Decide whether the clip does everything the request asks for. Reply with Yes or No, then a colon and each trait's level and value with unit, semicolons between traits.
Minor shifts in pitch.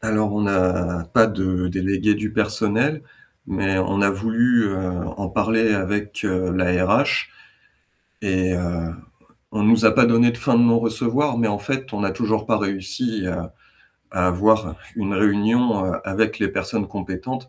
No: average, 3.0 semitones